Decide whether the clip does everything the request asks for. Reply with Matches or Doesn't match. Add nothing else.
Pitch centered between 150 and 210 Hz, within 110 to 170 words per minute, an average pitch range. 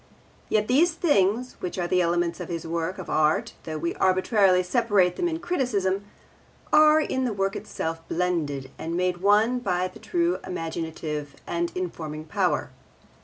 Matches